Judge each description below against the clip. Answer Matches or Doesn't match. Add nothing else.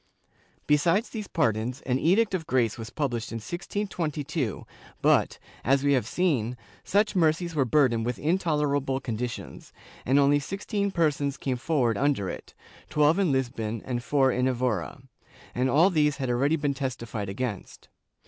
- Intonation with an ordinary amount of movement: Matches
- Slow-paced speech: Doesn't match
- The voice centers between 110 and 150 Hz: Matches